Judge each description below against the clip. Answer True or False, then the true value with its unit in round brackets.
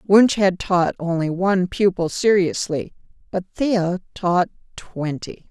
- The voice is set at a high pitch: False (180 Hz)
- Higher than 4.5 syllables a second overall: False (3.8 syllables/s)